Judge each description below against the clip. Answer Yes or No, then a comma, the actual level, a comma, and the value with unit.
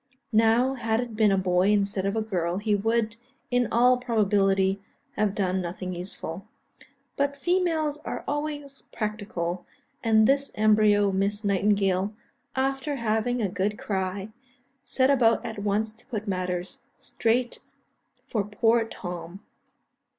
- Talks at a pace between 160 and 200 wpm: No, slow, 135 wpm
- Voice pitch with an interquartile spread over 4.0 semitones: No, average, 3.6 semitones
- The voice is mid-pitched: No, high, 215 Hz